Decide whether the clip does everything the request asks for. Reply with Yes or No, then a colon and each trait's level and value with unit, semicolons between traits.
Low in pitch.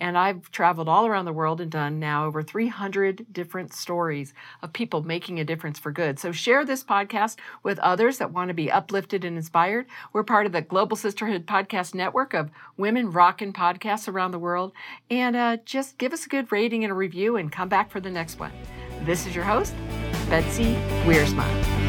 No: medium, 185 Hz